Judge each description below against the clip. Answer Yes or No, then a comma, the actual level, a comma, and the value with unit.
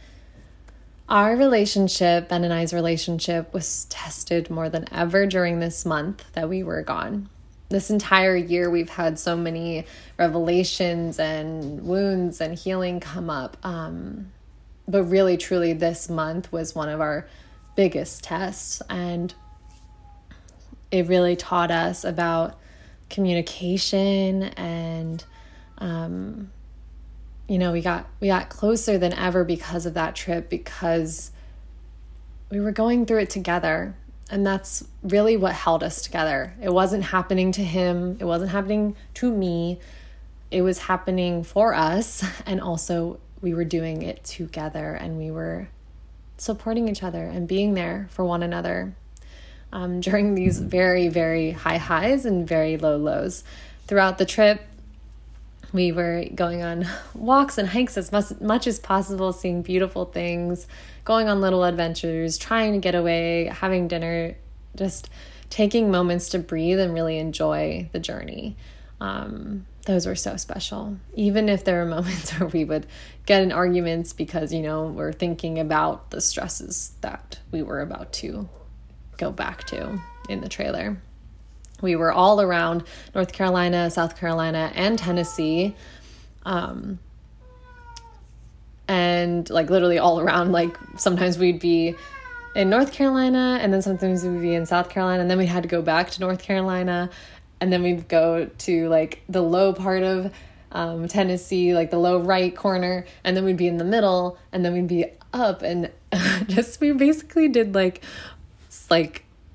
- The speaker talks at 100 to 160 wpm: Yes, average, 150 wpm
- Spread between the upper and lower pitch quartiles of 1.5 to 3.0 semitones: Yes, average, 2.7 semitones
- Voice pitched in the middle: Yes, medium, 175 Hz